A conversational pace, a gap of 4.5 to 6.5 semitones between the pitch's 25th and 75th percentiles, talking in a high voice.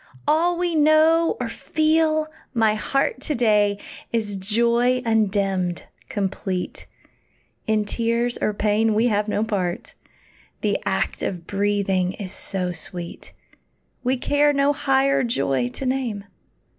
No: slow, 125 wpm; average, 5.3 semitones; high, 225 Hz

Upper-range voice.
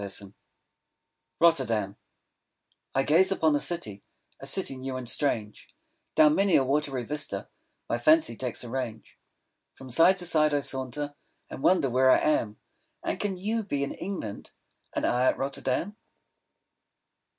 No: low, 135 Hz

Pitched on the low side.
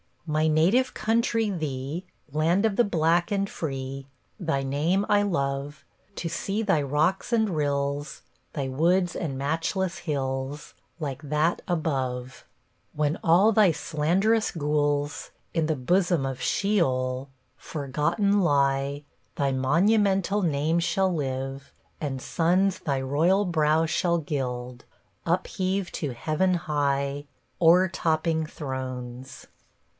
No: medium, 155 Hz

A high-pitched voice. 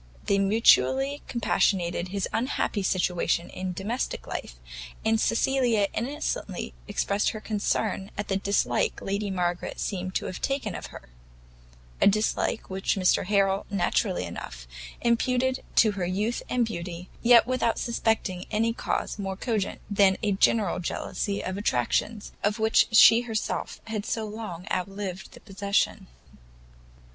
Yes: high, 200 Hz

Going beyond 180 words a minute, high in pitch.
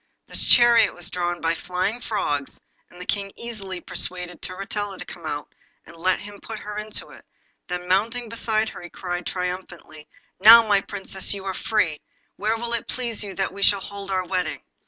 Yes: average, 190 wpm; high, 195 Hz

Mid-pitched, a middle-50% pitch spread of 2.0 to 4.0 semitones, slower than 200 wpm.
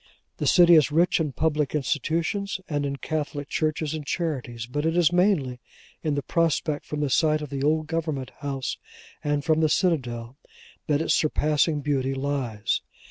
Yes: medium, 150 Hz; narrow, 2.4 semitones; average, 170 wpm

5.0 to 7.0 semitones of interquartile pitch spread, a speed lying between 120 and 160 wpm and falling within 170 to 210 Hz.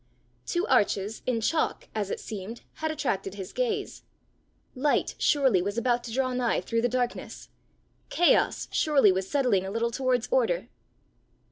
No: wide, 5.4 semitones; average, 150 wpm; high, 245 Hz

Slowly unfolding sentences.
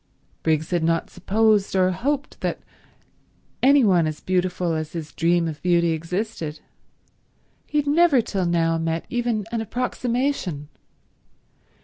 Yes: slow, 130 wpm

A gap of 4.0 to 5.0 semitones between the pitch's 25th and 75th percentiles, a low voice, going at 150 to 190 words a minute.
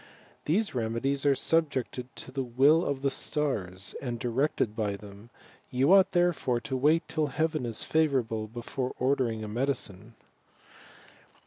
No: average, 4.5 semitones; low, 130 Hz; average, 140 wpm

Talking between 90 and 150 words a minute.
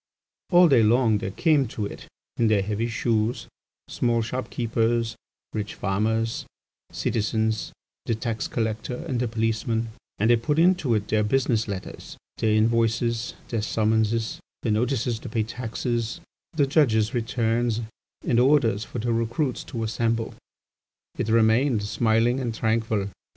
Yes: average, 140 wpm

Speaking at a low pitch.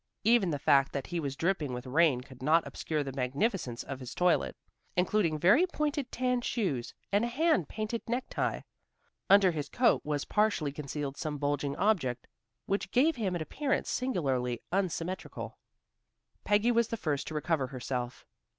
No: medium, 165 Hz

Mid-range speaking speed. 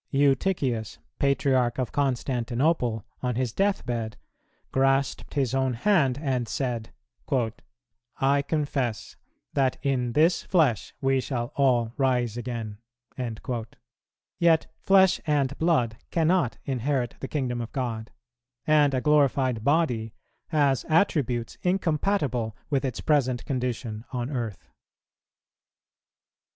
No: slow, 110 wpm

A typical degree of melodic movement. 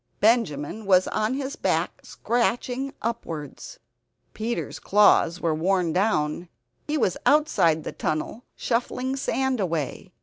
No: wide, 6.8 semitones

